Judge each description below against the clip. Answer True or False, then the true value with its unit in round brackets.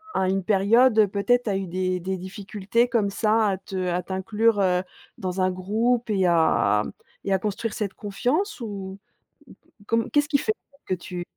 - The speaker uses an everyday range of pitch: True (3.4 semitones)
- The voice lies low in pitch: False (200 Hz)